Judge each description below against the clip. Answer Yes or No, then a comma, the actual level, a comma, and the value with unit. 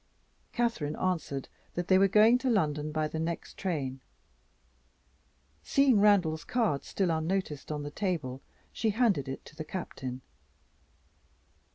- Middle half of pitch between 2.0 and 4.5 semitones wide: No, wide, 5.4 semitones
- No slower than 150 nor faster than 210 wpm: No, slow, 135 wpm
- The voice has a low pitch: No, medium, 170 Hz